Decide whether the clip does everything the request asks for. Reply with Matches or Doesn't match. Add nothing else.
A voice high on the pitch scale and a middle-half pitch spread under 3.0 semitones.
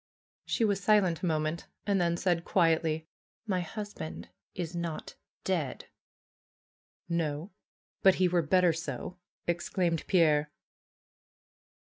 Doesn't match